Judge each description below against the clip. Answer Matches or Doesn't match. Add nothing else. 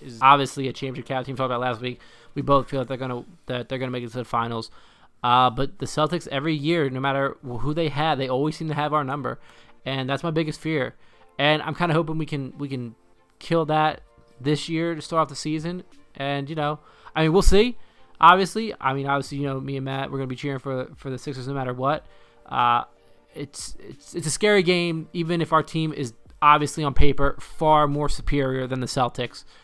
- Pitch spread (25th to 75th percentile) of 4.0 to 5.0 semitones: Doesn't match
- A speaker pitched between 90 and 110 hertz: Doesn't match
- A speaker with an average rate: Doesn't match